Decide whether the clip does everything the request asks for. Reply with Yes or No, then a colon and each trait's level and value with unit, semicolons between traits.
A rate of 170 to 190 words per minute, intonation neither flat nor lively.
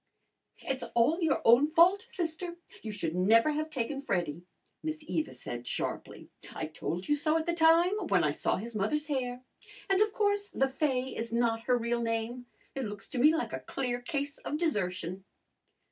No: average, 185 wpm; wide, 5.7 semitones